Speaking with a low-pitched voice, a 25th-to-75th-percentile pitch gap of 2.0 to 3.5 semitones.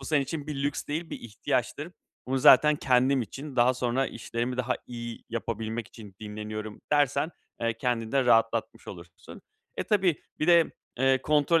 No: low, 125 Hz; average, 4.0 semitones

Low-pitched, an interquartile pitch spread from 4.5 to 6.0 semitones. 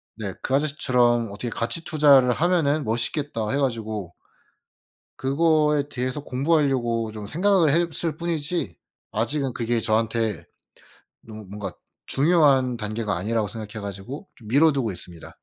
Yes: low, 125 Hz; average, 5.3 semitones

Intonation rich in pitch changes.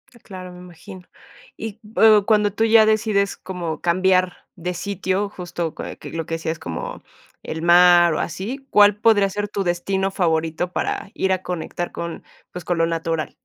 No: average, 2.9 semitones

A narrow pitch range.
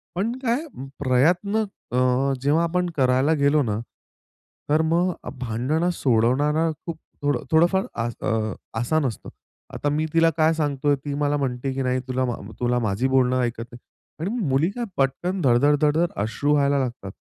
No: average, 4.3 semitones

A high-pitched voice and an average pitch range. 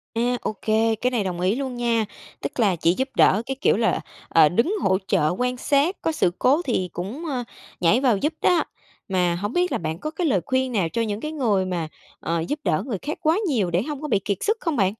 No: high, 230 Hz; wide, 6.8 semitones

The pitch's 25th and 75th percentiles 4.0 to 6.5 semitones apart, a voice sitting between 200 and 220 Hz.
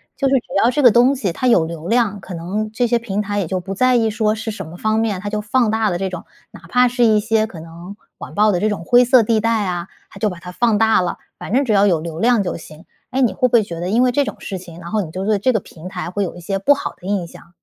Yes: average, 4.3 semitones; high, 210 Hz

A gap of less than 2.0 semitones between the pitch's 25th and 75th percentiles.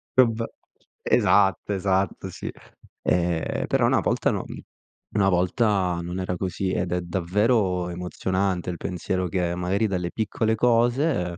No: average, 2.7 semitones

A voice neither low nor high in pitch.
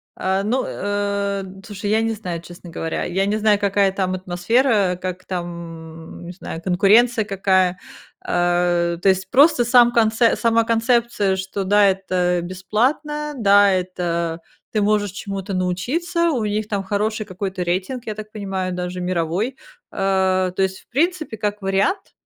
No: high, 195 Hz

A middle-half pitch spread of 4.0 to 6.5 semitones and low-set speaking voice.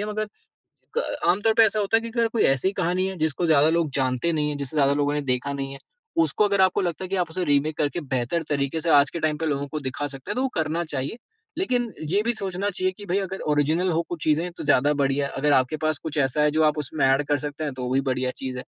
No: average, 4.7 semitones; medium, 155 Hz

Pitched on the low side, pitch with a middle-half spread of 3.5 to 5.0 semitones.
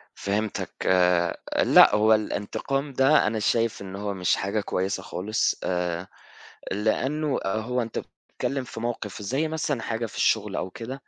Yes: low, 110 Hz; average, 4.5 semitones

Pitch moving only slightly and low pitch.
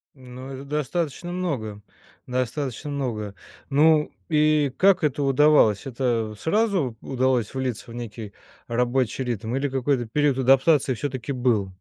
No: average, 3.6 semitones; low, 130 Hz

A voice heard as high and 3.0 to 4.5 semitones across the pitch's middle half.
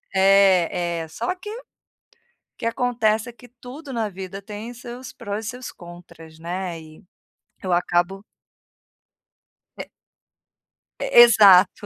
No: high, 200 Hz; average, 5.2 semitones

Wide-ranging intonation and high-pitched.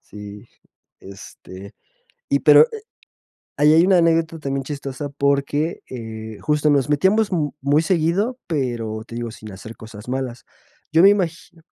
No: wide, 6.2 semitones; medium, 140 Hz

